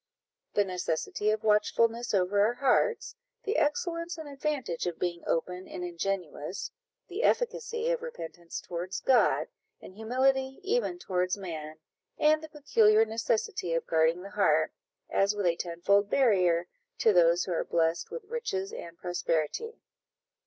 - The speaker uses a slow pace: No, average, 145 wpm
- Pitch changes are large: Yes, wide, 8.8 semitones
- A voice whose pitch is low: No, high, 205 Hz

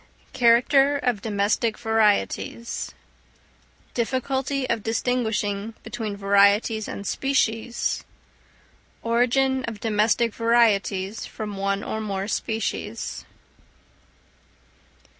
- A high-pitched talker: Yes, high, 225 Hz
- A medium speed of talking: No, slow, 80 wpm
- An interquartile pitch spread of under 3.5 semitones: Yes, narrow, 2.6 semitones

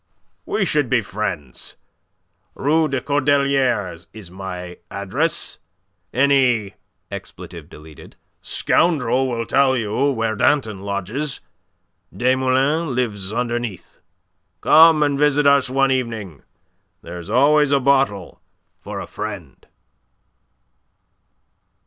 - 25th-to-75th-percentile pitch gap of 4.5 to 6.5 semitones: Yes, wide, 5.5 semitones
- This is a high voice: No, low, 125 Hz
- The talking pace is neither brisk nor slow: No, slow, 95 wpm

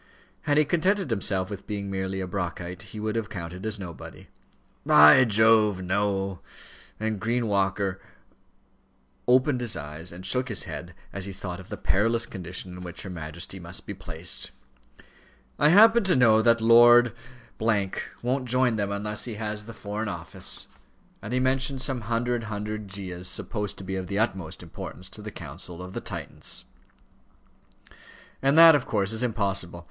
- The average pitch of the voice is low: Yes, low, 105 Hz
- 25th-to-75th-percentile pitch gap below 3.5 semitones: No, average, 3.9 semitones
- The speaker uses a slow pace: No, average, 165 wpm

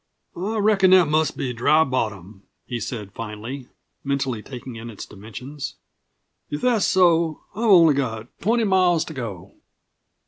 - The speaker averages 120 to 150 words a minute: Yes, average, 145 wpm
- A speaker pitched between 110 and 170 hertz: Yes, medium, 140 Hz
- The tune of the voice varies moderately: No, wide, 7.7 semitones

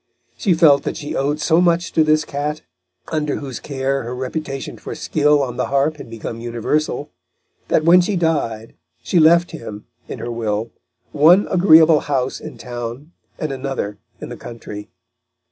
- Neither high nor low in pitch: Yes, medium, 145 Hz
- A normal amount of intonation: Yes, average, 4.6 semitones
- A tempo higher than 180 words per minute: No, average, 165 wpm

